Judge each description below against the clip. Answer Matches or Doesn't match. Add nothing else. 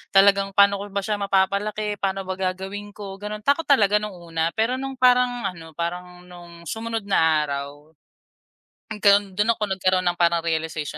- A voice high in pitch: Matches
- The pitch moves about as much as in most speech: Matches